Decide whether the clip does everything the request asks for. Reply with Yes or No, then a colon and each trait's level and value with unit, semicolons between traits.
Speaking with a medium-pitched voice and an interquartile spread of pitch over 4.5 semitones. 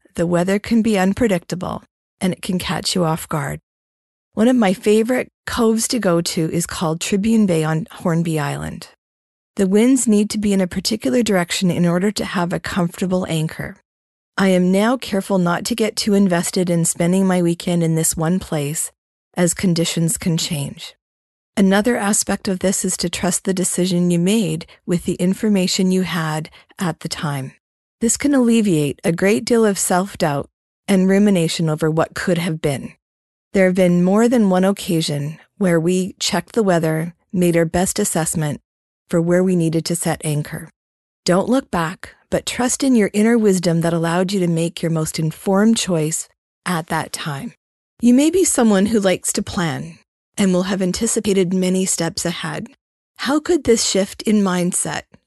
No: medium, 180 Hz; average, 3.6 semitones